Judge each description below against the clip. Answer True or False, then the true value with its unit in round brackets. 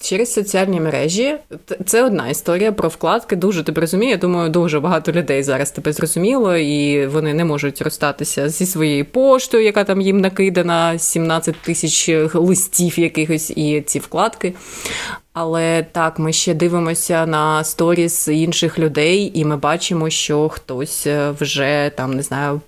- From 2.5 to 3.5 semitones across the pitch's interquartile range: True (3.2 semitones)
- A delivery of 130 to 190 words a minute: True (150 wpm)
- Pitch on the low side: False (165 Hz)